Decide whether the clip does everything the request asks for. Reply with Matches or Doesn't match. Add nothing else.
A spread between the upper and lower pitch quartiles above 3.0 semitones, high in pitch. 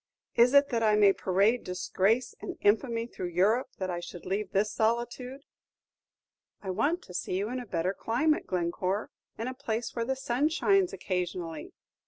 Matches